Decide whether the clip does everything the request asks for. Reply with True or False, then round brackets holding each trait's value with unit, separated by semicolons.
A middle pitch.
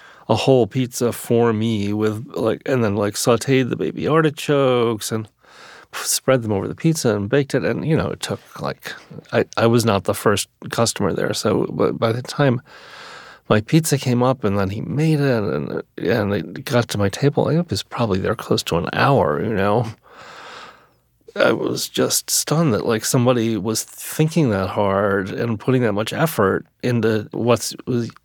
False (120 Hz)